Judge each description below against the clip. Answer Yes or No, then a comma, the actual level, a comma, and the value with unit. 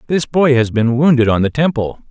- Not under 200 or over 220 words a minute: No, fast, 230 wpm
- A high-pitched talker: No, low, 130 Hz